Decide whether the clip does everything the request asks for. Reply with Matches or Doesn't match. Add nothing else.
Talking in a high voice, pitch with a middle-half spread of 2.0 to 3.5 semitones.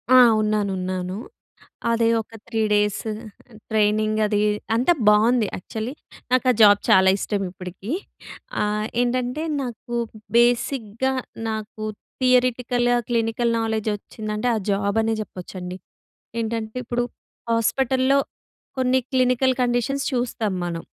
Matches